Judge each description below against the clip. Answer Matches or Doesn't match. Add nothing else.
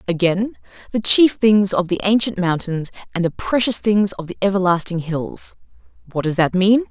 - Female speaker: Matches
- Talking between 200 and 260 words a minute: Doesn't match